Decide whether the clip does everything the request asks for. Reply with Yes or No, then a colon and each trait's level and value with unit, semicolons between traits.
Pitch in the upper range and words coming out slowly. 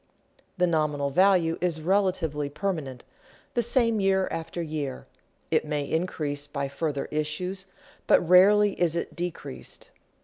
No: medium, 165 Hz; slow, 130 wpm